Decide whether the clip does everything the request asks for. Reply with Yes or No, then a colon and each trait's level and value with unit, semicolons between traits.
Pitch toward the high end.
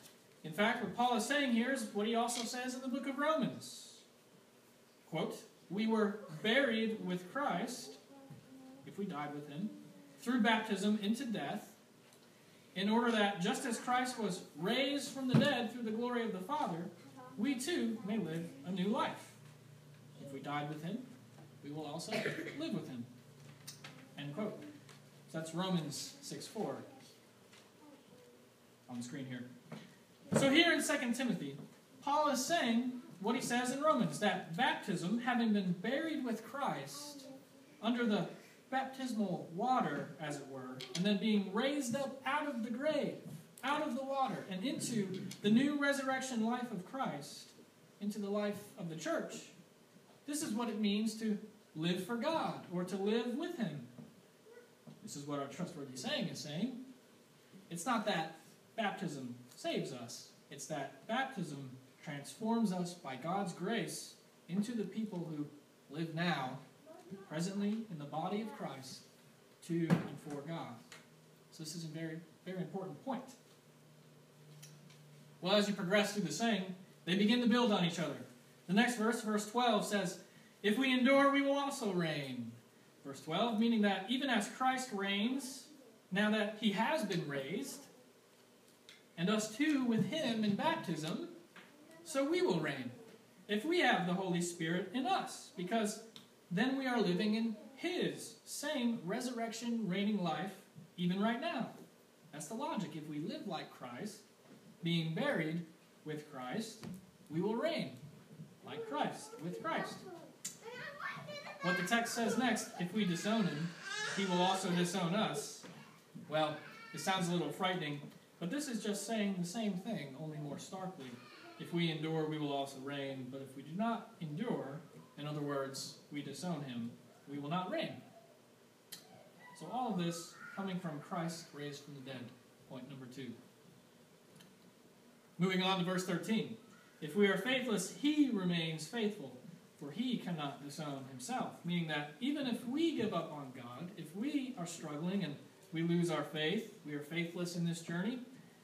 Yes: high, 200 Hz